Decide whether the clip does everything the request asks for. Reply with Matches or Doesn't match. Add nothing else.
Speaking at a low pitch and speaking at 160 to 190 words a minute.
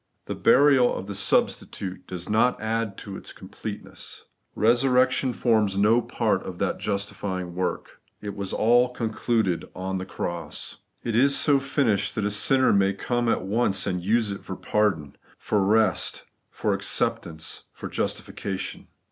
Doesn't match